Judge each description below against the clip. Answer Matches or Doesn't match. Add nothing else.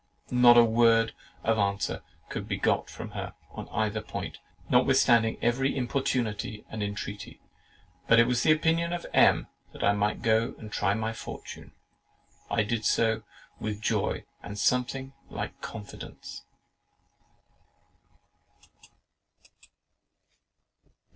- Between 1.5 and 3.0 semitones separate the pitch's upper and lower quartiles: Matches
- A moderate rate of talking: Doesn't match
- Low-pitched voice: Matches